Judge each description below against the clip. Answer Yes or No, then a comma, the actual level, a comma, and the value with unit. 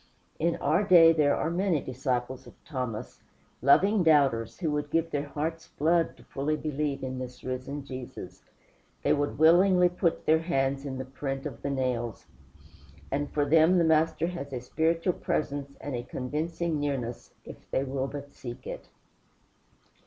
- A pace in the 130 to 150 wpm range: No, average, 165 wpm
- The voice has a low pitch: No, medium, 145 Hz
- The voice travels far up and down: No, average, 3.6 semitones